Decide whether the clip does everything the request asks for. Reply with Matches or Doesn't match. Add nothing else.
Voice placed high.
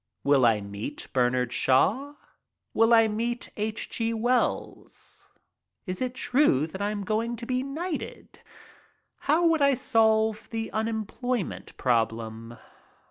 Matches